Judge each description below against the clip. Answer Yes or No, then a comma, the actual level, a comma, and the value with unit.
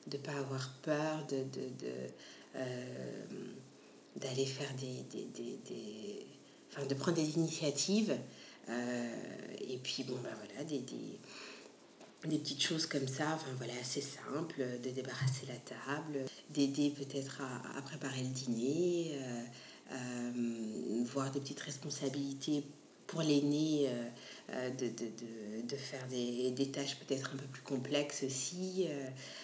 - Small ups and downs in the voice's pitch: Yes, narrow, 2.2 semitones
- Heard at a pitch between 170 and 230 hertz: No, low, 135 Hz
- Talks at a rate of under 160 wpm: Yes, slow, 145 wpm